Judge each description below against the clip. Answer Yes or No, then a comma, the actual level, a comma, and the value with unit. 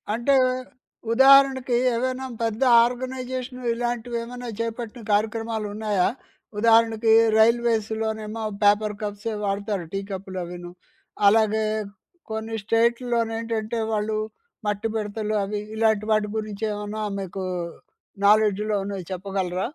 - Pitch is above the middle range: Yes, high, 220 Hz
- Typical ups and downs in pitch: No, narrow, 2.1 semitones